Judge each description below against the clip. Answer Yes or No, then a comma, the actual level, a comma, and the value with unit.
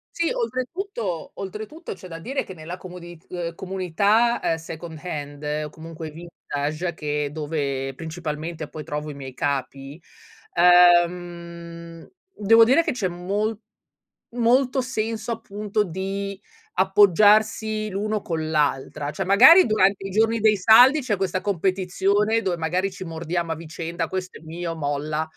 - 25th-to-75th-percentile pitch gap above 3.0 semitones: Yes, average, 4.7 semitones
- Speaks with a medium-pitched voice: Yes, medium, 180 Hz